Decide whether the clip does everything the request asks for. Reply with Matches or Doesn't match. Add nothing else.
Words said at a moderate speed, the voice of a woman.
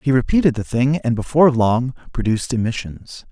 Doesn't match